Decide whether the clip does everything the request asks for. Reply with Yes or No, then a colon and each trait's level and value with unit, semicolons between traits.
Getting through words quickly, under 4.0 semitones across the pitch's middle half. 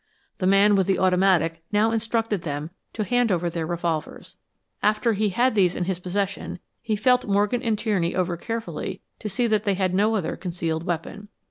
No: average, 190 wpm; average, 3.6 semitones